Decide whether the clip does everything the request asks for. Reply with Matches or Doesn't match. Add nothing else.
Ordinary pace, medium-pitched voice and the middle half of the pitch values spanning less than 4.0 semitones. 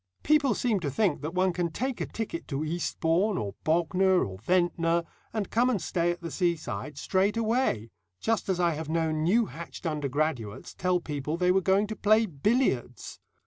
Doesn't match